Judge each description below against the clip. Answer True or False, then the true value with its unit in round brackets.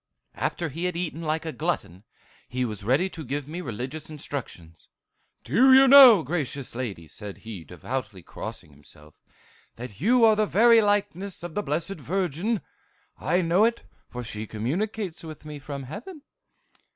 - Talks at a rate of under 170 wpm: True (160 wpm)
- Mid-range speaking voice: True (155 Hz)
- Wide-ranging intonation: True (7.9 semitones)